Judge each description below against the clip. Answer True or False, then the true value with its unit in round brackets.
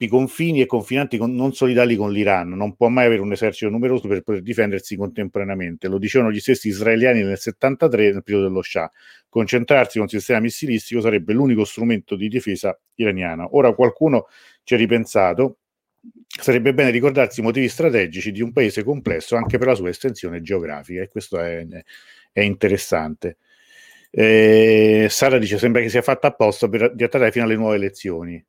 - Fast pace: True (175 wpm)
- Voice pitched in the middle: False (115 Hz)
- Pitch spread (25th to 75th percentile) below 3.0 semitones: False (3.8 semitones)